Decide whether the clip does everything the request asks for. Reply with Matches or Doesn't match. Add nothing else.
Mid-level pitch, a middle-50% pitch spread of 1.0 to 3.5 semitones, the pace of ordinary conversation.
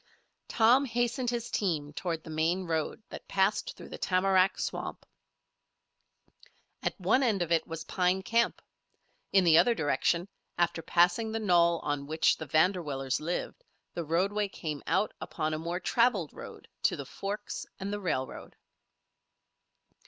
Doesn't match